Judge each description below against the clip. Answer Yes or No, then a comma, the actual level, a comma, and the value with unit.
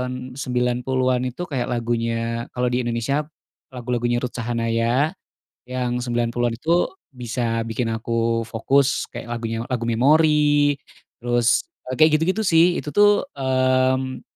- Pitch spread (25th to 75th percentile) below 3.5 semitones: Yes, narrow, 2.6 semitones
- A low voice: Yes, low, 125 Hz